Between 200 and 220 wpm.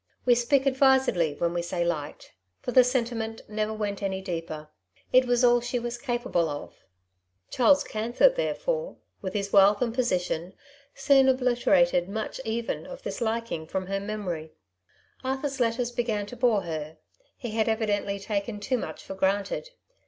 No: average, 160 wpm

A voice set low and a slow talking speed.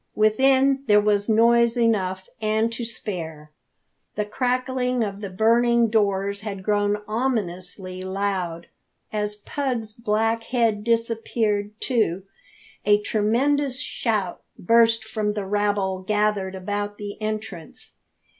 No: high, 210 Hz; slow, 115 wpm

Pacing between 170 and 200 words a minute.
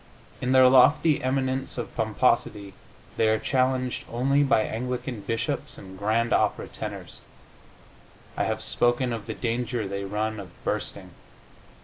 No: slow, 135 wpm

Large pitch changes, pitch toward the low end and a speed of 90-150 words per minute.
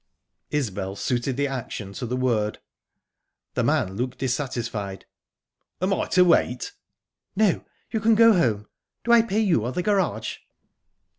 Yes: wide, 8.6 semitones; low, 130 Hz; average, 145 wpm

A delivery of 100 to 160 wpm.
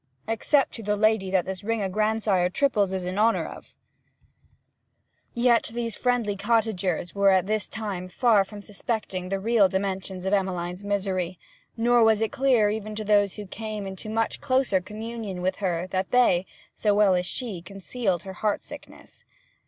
No: average, 170 wpm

